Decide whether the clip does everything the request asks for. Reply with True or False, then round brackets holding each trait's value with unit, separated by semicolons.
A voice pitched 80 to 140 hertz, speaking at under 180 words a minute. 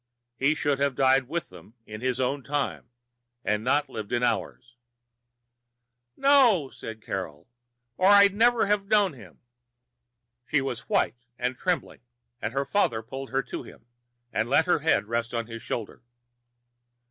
True (135 Hz; 155 wpm)